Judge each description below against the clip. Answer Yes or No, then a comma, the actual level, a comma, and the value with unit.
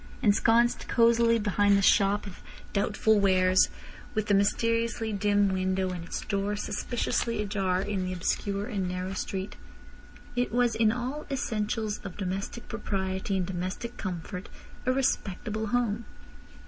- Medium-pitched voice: No, high, 205 Hz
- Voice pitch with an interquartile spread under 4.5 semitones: Yes, average, 3.3 semitones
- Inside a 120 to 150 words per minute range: Yes, slow, 135 wpm